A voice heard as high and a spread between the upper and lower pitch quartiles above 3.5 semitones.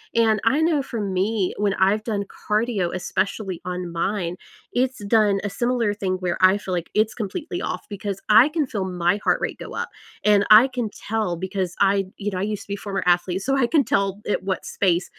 No: high, 200 Hz; average, 3.0 semitones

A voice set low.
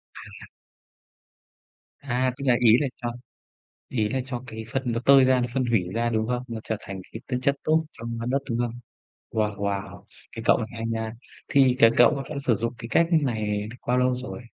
Yes: low, 120 Hz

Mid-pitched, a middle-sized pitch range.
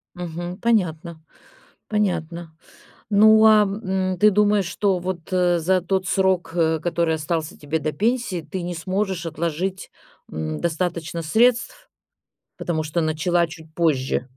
Yes: medium, 175 Hz; average, 3.0 semitones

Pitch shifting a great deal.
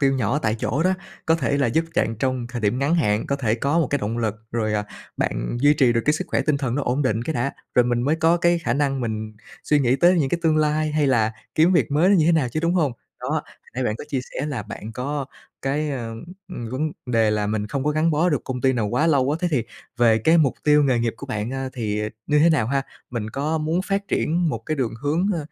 No: average, 4.6 semitones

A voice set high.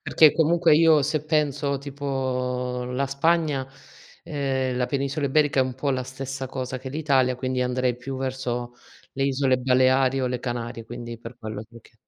No: low, 130 Hz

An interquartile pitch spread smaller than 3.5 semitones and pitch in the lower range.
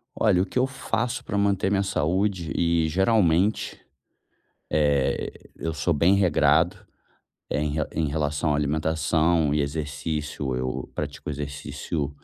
No: average, 4.2 semitones; very low, 80 Hz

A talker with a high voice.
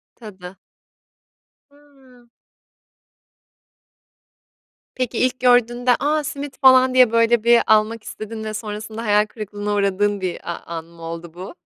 Yes: high, 220 Hz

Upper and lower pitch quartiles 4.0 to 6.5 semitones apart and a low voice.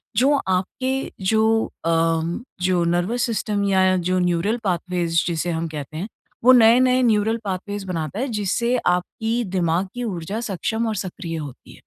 No: average, 4.4 semitones; high, 190 Hz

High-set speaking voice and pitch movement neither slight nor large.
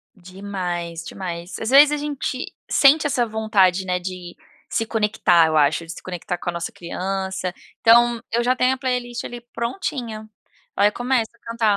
Yes: high, 210 Hz; average, 5.0 semitones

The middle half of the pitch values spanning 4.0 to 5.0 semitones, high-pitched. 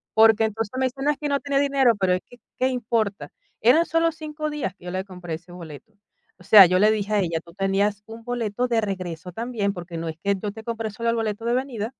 Yes: average, 4.5 semitones; high, 220 Hz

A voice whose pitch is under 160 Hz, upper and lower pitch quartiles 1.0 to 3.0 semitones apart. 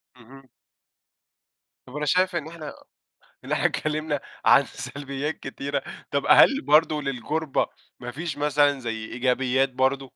Yes: medium, 140 Hz; narrow, 2.5 semitones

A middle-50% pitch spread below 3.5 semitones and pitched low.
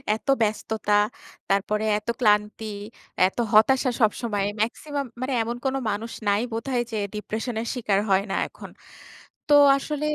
No: average, 3.0 semitones; high, 220 Hz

